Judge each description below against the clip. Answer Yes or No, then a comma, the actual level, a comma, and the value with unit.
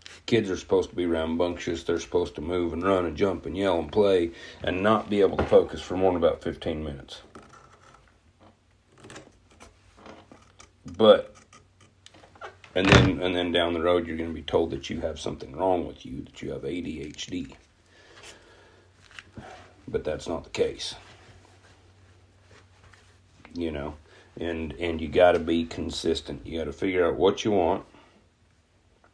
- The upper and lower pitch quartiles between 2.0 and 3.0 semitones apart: Yes, narrow, 2.4 semitones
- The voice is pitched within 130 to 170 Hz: No, very low, 90 Hz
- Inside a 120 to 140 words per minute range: No, average, 155 wpm